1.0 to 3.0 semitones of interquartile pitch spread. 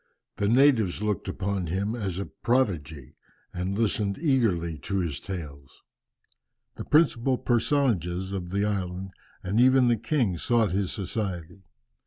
No: average, 4.7 semitones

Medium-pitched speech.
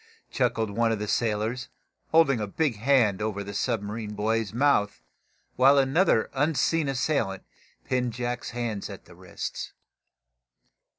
No: low, 115 Hz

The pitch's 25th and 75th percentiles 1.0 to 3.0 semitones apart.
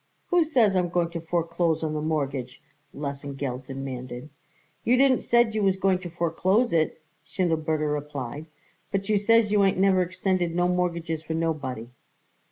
No: average, 4.3 semitones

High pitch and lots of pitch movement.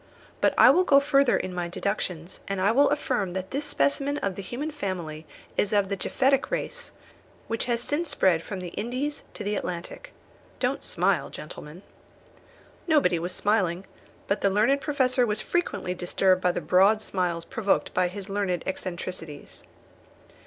Yes: high, 200 Hz; wide, 6.6 semitones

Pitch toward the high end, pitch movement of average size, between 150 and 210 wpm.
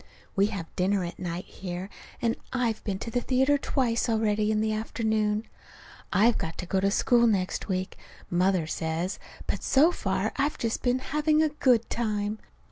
Yes: high, 215 Hz; average, 4.2 semitones; average, 175 wpm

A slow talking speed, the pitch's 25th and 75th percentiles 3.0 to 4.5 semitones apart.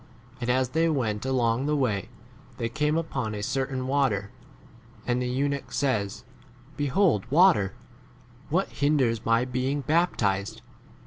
Yes: slow, 130 wpm; average, 4.0 semitones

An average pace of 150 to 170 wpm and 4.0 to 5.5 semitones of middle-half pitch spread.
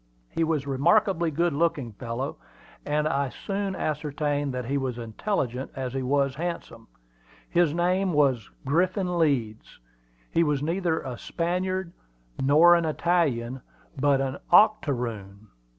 No: slow, 135 wpm; average, 4.7 semitones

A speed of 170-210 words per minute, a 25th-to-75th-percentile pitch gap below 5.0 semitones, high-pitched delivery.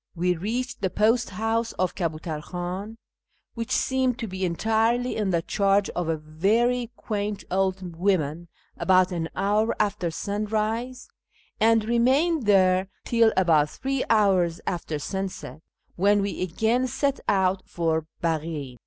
No: slow, 135 wpm; average, 4.4 semitones; high, 195 Hz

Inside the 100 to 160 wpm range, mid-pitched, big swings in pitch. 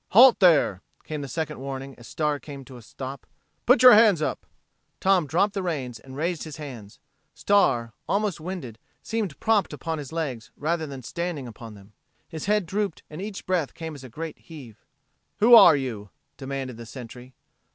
No: average, 185 wpm; medium, 150 Hz; wide, 5.9 semitones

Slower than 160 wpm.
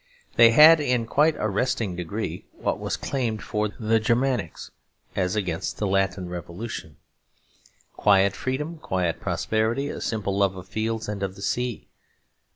Yes: average, 145 wpm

